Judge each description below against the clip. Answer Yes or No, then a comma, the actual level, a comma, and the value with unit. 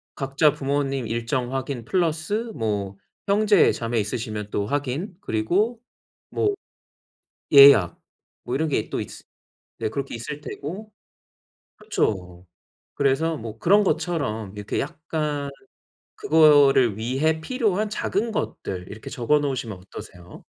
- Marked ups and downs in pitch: Yes, wide, 6.3 semitones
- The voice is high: No, medium, 140 Hz